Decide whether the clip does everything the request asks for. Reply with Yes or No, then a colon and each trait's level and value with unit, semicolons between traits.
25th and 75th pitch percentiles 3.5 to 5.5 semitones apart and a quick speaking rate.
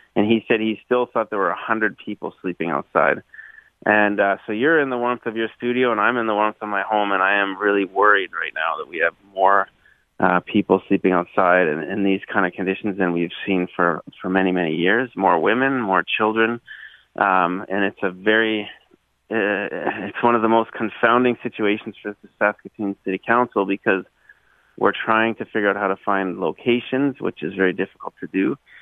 No: average, 2.9 semitones; fast, 215 wpm